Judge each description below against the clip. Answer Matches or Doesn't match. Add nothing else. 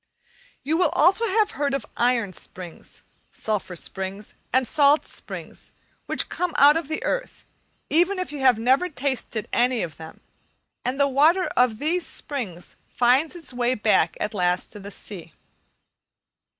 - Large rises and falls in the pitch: Matches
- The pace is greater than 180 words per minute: Doesn't match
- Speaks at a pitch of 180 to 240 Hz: Doesn't match